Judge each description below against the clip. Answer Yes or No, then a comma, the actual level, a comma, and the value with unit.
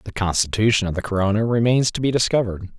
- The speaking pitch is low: Yes, low, 110 Hz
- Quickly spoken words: No, average, 195 wpm